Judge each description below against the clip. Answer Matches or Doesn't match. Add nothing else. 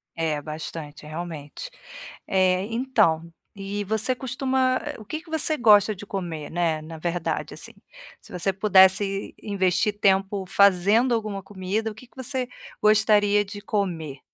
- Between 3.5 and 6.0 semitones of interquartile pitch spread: Matches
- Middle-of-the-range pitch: Doesn't match